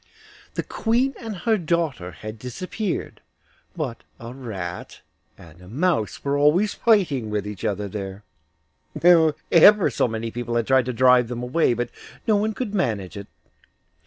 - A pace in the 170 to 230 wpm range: No, average, 155 wpm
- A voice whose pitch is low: Yes, low, 125 Hz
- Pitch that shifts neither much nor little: No, wide, 8.7 semitones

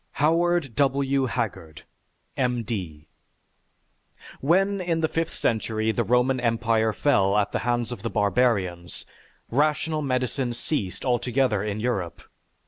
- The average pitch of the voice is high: No, low, 120 Hz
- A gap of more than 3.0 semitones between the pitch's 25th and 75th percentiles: Yes, average, 4.4 semitones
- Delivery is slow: Yes, slow, 125 wpm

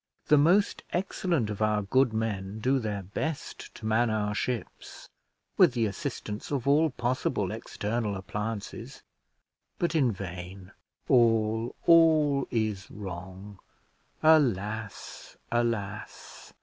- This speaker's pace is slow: Yes, slow, 110 wpm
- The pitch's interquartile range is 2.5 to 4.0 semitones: No, average, 4.8 semitones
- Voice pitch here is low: Yes, low, 110 Hz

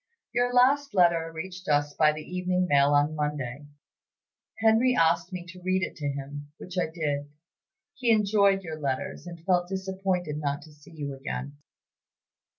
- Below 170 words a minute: Yes, average, 160 wpm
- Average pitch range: Yes, average, 4.4 semitones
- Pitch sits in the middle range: Yes, medium, 165 Hz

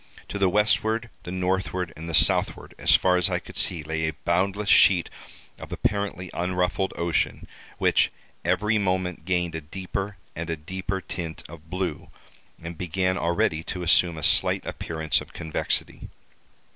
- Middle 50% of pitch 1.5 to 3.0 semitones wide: Yes, narrow, 2.4 semitones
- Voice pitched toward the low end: Yes, very low, 90 Hz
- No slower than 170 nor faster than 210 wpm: No, average, 160 wpm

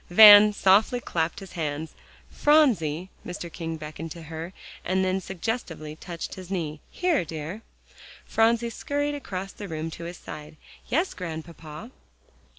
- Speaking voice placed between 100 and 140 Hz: No, medium, 180 Hz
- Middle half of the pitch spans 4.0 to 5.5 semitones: Yes, average, 4.9 semitones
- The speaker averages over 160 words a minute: No, average, 140 wpm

